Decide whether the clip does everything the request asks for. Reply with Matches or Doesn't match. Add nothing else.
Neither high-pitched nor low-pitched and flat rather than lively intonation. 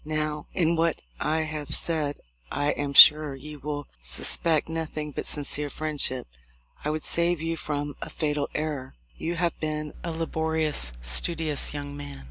Matches